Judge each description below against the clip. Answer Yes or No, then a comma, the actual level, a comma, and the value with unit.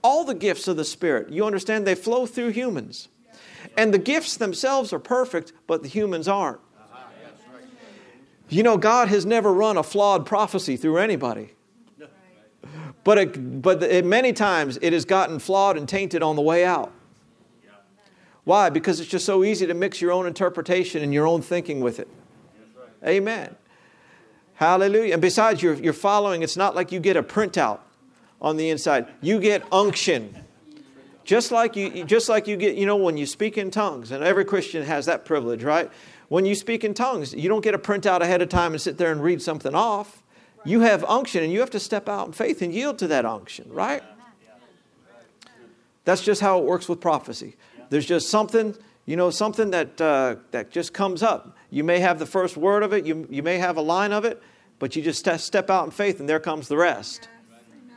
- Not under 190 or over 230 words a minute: Yes, average, 200 wpm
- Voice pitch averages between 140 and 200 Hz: Yes, high, 190 Hz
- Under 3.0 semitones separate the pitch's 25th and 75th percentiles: No, average, 4.1 semitones